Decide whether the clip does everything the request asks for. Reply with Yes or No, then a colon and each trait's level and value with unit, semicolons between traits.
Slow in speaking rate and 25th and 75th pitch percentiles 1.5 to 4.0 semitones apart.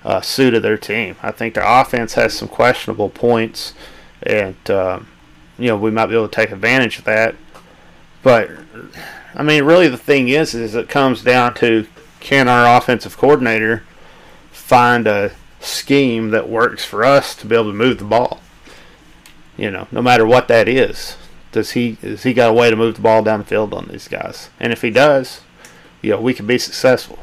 No: average, 200 wpm; narrow, 2.4 semitones